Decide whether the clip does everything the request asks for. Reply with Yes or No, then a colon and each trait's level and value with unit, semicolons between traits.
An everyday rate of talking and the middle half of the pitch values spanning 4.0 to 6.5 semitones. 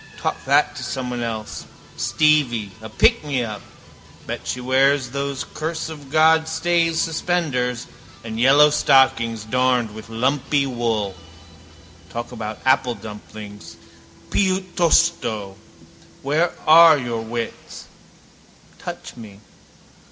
No: slow, 105 wpm; average, 5.3 semitones